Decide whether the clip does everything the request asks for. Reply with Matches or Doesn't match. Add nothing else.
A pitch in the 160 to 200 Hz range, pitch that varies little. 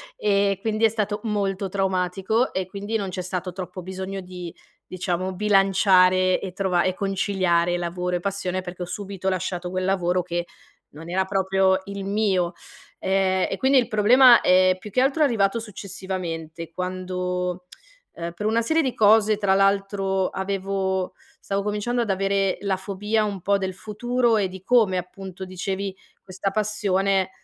Matches